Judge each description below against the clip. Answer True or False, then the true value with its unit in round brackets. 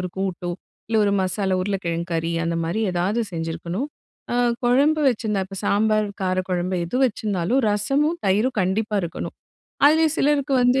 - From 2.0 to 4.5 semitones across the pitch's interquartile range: False (5.3 semitones)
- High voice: True (205 Hz)